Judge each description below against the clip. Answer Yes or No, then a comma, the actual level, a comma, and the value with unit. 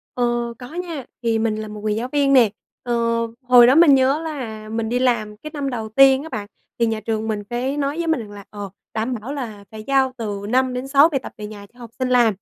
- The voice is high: Yes, high, 240 Hz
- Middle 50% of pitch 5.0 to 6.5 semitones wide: No, average, 3.7 semitones